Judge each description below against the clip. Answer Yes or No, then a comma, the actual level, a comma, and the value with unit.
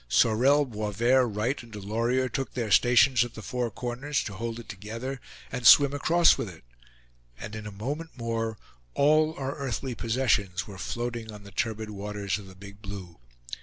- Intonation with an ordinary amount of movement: Yes, average, 3.8 semitones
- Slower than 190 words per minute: Yes, average, 175 wpm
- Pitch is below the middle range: Yes, low, 115 Hz